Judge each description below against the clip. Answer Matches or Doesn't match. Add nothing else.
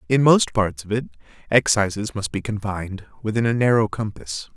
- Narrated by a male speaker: Matches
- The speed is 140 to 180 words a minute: Matches